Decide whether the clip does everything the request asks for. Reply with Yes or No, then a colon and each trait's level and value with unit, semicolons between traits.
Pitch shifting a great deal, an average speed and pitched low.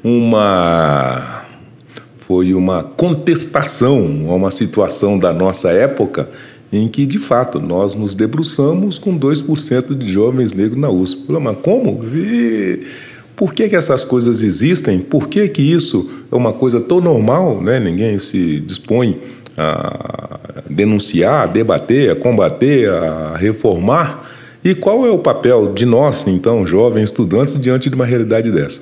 Yes: wide, 6.6 semitones; average, 145 wpm; low, 115 Hz